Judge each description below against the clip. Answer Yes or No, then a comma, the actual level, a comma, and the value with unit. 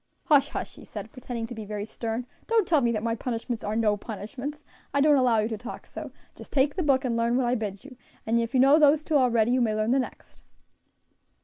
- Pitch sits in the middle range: No, high, 245 Hz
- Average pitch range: Yes, average, 3.7 semitones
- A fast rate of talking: Yes, fast, 245 wpm